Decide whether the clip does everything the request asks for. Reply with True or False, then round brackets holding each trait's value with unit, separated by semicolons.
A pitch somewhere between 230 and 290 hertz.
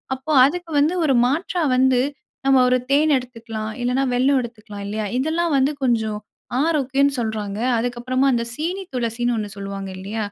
True (250 Hz)